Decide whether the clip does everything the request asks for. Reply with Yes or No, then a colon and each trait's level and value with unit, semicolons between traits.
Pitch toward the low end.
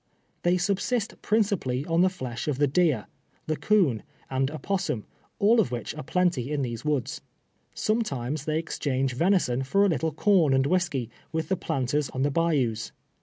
No: medium, 150 Hz